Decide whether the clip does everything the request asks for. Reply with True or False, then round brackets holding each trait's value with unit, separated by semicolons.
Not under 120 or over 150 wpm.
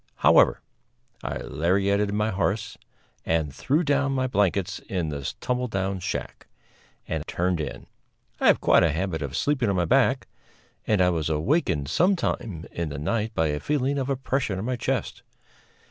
False (170 wpm)